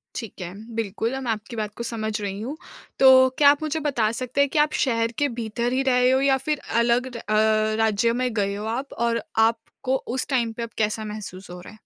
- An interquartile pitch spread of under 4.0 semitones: Yes, average, 3.2 semitones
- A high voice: Yes, high, 230 Hz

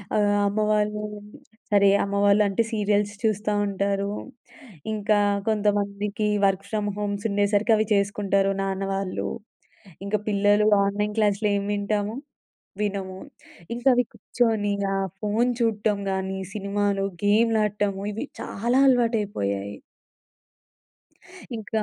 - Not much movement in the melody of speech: Yes, narrow, 1.1 semitones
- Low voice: No, high, 205 Hz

